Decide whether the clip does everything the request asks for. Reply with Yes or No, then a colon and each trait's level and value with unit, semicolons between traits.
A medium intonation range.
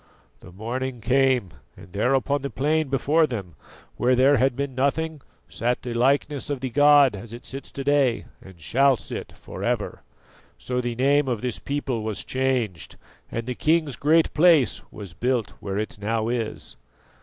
Yes: average, 3.5 semitones